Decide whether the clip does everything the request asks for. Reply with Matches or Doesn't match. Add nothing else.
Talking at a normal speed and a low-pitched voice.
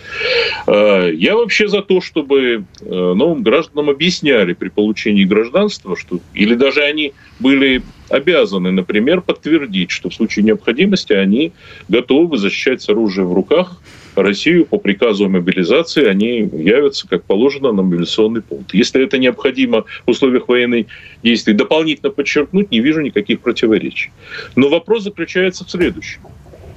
Matches